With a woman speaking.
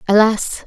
Yes: female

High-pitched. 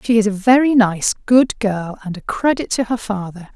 Yes: high, 215 Hz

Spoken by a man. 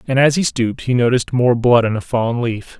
Yes: male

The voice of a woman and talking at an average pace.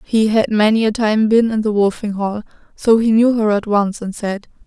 No: female; fast, 230 wpm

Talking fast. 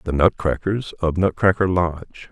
No: slow, 130 wpm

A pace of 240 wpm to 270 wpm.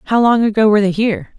Yes: fast, 260 wpm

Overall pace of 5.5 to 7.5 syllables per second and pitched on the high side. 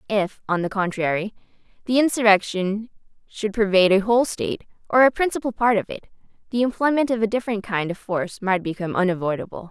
Yes: 6.4 syllables/s; high, 205 Hz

